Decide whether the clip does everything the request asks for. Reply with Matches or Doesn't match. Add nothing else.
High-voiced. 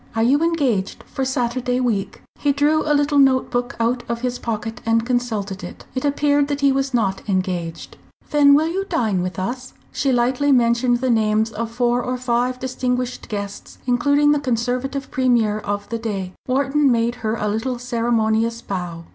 Matches